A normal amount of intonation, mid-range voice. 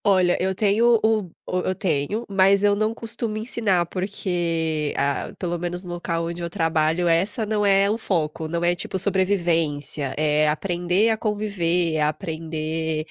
Yes: average, 3.8 semitones; medium, 175 Hz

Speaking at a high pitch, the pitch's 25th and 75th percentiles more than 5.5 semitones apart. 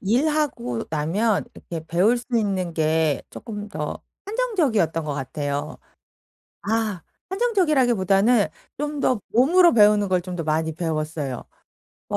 Yes: high, 200 Hz; wide, 7.5 semitones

